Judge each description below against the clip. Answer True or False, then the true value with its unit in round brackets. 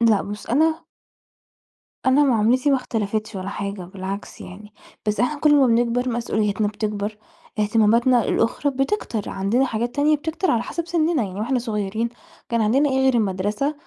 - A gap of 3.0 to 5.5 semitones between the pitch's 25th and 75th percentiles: True (4.1 semitones)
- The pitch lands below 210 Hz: False (230 Hz)